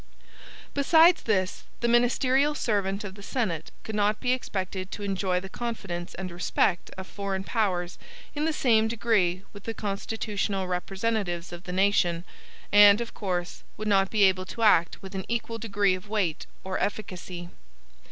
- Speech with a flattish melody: No, average, 3.2 semitones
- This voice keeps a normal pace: Yes, average, 160 wpm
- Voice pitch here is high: Yes, high, 200 Hz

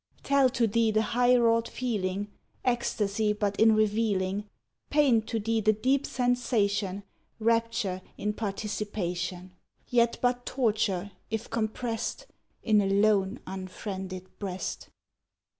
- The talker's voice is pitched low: No, high, 215 Hz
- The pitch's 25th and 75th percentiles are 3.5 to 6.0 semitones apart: No, average, 2.7 semitones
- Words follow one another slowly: Yes, slow, 115 wpm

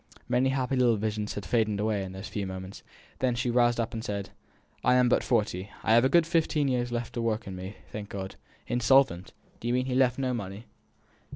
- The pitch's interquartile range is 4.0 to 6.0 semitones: No, average, 3.6 semitones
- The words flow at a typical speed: No, fast, 225 wpm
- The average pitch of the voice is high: No, low, 115 Hz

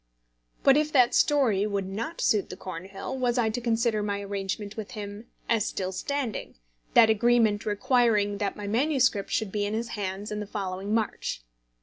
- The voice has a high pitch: Yes, high, 210 Hz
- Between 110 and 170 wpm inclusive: No, average, 180 wpm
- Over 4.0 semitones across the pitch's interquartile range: No, average, 2.9 semitones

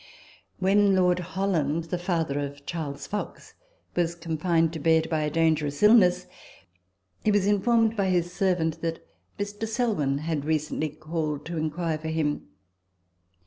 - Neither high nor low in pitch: Yes, medium, 165 Hz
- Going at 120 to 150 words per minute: Yes, average, 145 wpm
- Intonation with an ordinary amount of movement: Yes, average, 3.5 semitones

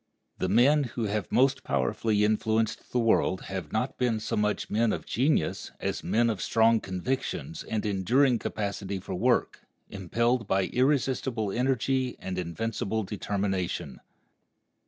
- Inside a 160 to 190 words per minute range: No, slow, 135 wpm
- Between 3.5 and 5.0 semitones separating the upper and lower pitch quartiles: Yes, average, 4.2 semitones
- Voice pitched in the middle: No, low, 110 Hz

